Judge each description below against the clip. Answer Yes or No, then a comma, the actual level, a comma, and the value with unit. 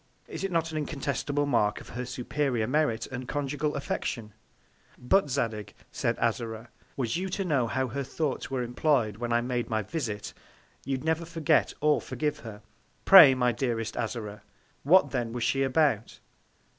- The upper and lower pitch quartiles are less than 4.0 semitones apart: No, average, 4.3 semitones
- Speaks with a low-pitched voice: Yes, low, 130 Hz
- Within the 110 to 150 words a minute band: No, average, 165 wpm